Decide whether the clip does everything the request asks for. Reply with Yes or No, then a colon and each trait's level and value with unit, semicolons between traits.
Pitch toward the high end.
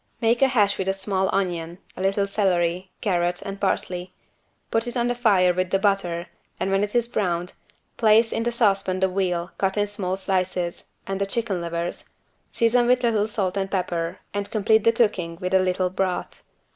Yes: high, 195 Hz